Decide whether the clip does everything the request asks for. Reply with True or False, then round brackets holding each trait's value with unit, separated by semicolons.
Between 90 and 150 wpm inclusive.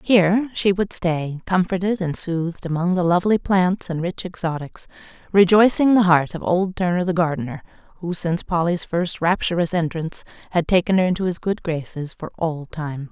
False (175 wpm)